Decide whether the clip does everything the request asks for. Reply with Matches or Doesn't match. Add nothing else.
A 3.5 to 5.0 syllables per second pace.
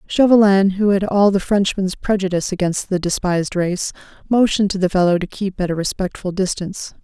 Doesn't match